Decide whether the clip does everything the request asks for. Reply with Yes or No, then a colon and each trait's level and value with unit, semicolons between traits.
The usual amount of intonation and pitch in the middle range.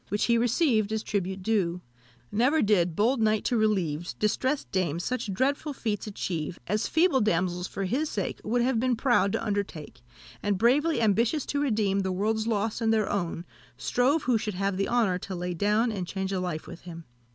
No: average, 4.2 semitones; high, 210 Hz